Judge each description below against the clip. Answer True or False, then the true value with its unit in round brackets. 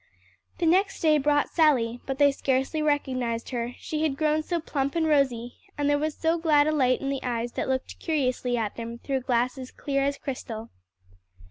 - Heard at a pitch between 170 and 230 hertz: False (275 Hz)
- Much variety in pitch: False (3.5 semitones)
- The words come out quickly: False (195 wpm)